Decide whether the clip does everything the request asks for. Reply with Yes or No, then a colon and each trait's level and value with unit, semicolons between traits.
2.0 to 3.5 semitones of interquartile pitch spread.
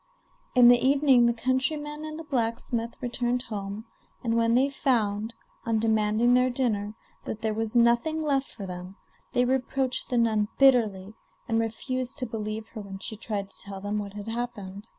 Yes: average, 3.2 semitones